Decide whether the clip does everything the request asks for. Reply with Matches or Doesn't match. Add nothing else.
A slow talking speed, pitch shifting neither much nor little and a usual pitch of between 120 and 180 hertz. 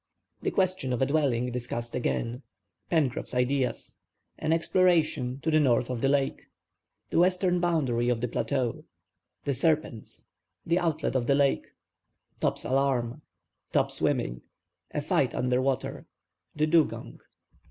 Matches